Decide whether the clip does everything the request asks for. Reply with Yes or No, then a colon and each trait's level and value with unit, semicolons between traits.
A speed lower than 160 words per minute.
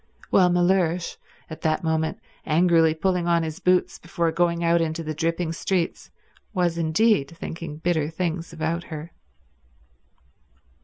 Yes: slow, 135 wpm